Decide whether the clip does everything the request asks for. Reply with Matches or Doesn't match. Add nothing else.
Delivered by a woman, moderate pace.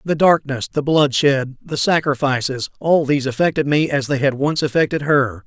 Doesn't match